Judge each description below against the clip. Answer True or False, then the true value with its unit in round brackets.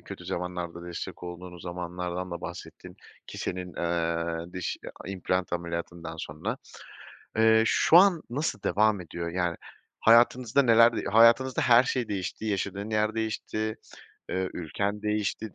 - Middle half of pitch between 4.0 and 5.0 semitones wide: True (4.3 semitones)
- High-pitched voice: False (95 Hz)